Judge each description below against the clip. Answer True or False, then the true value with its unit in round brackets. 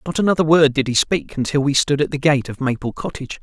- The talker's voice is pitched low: False (145 Hz)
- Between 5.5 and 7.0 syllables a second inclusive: True (6.3 syllables/s)